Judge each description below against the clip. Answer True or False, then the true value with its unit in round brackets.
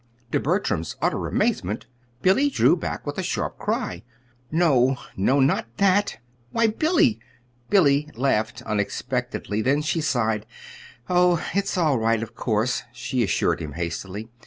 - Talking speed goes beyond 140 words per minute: False (135 wpm)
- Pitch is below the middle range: True (130 Hz)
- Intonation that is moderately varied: False (8.1 semitones)